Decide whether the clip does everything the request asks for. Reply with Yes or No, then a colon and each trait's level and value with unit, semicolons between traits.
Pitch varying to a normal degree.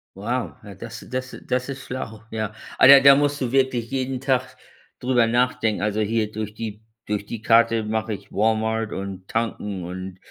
Yes: average, 3.2 semitones